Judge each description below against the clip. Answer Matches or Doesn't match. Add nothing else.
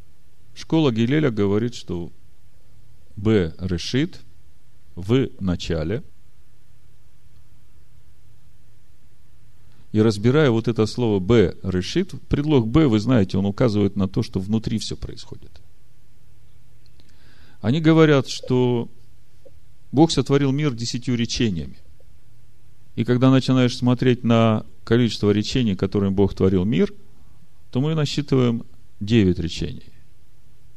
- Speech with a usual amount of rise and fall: Matches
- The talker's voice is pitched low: Matches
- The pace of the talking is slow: Matches